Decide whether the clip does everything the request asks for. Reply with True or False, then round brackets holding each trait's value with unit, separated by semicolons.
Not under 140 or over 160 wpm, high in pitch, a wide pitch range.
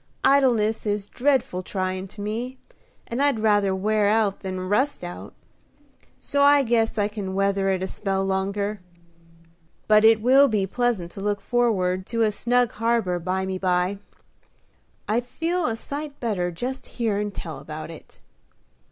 False (150 wpm; 210 Hz; 3.9 semitones)